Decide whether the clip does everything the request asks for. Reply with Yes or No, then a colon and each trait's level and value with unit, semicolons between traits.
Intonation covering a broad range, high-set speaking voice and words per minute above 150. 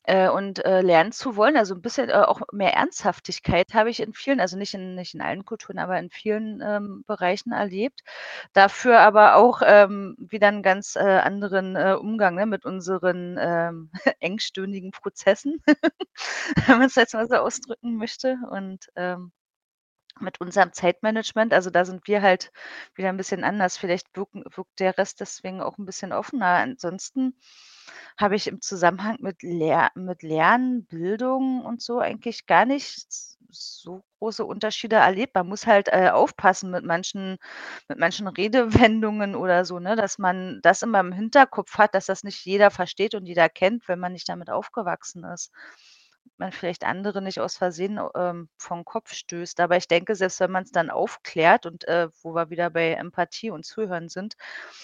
No: average, 3.5 semitones; high, 195 Hz; average, 175 wpm